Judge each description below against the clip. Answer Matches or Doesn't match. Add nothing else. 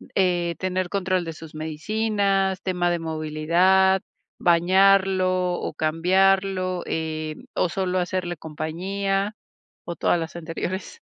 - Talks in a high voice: Doesn't match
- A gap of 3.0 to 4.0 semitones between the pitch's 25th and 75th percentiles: Doesn't match